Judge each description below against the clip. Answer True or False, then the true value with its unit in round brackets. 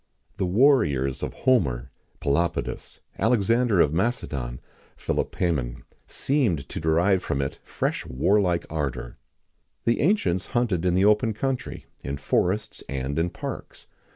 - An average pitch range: False (8.1 semitones)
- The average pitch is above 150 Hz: False (90 Hz)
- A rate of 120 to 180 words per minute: True (140 wpm)